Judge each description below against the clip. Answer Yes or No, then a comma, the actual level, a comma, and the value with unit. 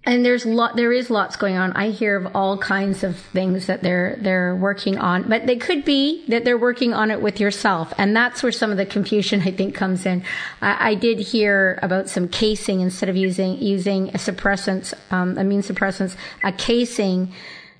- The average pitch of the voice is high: Yes, high, 200 Hz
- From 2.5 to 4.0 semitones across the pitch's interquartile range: Yes, average, 2.8 semitones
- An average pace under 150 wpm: No, average, 200 wpm